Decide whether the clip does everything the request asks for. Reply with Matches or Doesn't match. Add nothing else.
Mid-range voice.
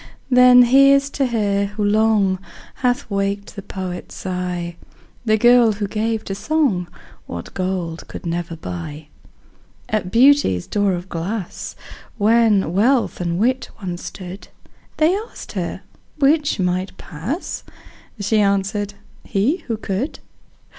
Doesn't match